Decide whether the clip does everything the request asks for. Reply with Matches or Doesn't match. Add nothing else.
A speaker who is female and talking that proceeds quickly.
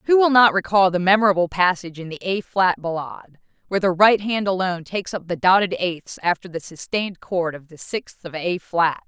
Matches